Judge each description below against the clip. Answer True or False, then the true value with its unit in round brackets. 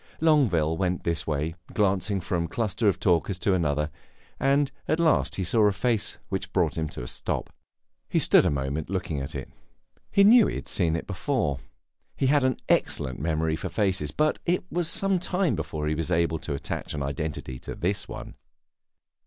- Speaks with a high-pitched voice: False (90 Hz)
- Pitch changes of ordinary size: False (8.3 semitones)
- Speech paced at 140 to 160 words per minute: False (195 wpm)